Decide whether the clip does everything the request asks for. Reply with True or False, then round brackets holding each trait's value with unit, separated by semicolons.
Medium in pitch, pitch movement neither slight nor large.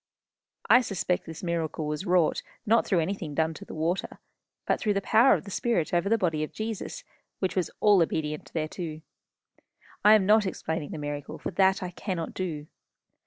True (180 Hz; 4.0 semitones)